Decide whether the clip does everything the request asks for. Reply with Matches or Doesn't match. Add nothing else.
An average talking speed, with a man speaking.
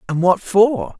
Matches